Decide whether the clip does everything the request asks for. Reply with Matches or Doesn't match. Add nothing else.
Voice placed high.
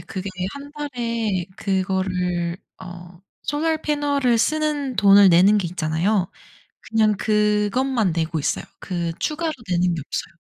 Matches